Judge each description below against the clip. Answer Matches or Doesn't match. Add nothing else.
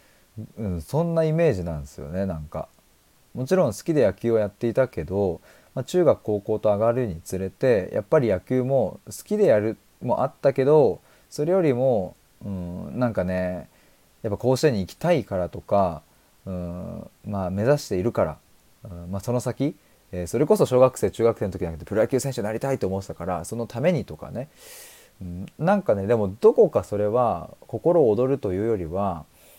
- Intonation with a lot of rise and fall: Matches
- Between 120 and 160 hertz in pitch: Doesn't match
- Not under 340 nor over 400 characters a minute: Matches